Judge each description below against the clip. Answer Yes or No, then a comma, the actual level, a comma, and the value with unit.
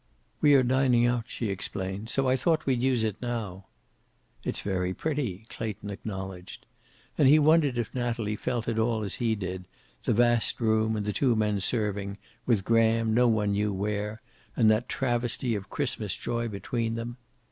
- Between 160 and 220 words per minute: Yes, average, 175 wpm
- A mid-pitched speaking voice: No, low, 115 Hz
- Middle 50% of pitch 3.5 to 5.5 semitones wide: No, average, 2.8 semitones